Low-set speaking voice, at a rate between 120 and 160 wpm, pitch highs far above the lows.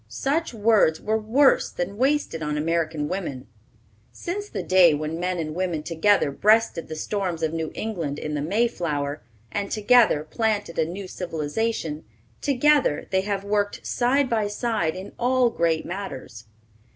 No: medium, 185 Hz; average, 150 wpm; wide, 5.9 semitones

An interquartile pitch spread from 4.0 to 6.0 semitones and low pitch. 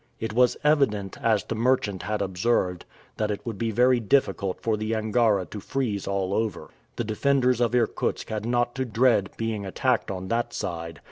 No: average, 3.3 semitones; low, 110 Hz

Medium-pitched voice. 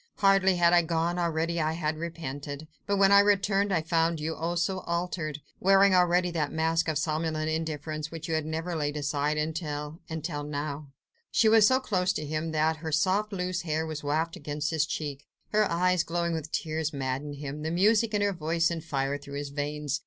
Yes: medium, 160 Hz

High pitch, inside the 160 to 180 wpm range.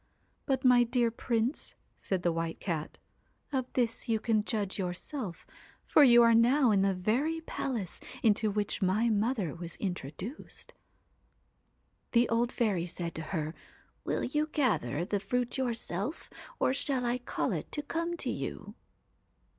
No: high, 230 Hz; average, 150 wpm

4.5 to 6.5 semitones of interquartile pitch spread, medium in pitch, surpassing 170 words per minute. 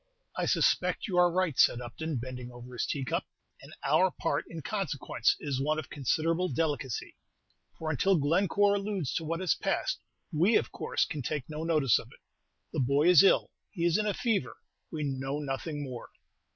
Yes: average, 4.8 semitones; medium, 155 Hz; average, 185 wpm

